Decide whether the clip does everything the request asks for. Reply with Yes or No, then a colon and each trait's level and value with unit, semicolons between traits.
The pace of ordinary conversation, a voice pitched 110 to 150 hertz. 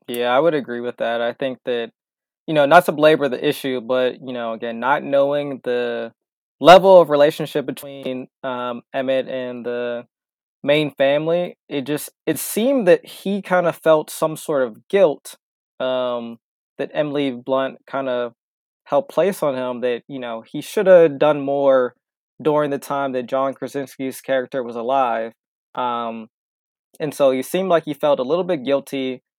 Yes: average, 175 wpm; low, 135 Hz